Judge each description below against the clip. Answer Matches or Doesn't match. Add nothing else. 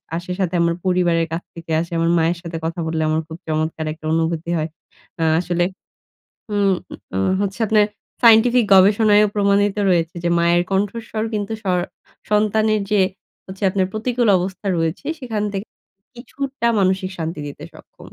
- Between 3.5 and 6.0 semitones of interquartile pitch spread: Matches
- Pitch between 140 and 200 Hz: Matches